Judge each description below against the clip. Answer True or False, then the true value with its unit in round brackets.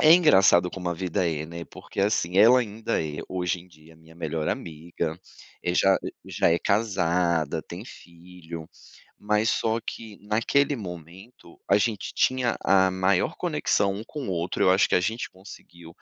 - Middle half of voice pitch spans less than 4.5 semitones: True (3.9 semitones)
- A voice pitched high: False (90 Hz)